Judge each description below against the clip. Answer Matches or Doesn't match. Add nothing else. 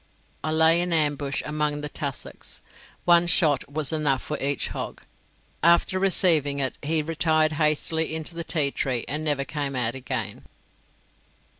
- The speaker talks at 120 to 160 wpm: Matches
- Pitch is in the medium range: Matches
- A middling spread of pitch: Doesn't match